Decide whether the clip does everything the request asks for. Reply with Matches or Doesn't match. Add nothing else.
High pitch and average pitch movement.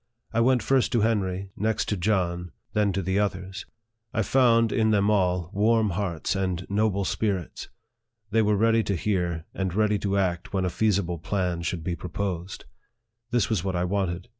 Doesn't match